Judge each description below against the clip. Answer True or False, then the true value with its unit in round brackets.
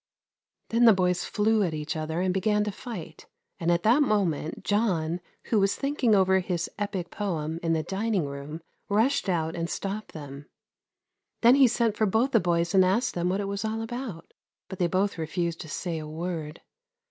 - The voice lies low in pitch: False (185 Hz)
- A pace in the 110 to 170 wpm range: False (195 wpm)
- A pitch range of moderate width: True (4.4 semitones)